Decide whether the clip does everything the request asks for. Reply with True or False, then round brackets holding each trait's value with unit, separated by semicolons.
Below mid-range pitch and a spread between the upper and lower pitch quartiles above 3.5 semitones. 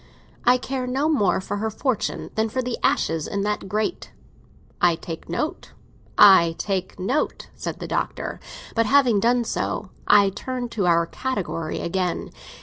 False (210 Hz; 5.2 semitones)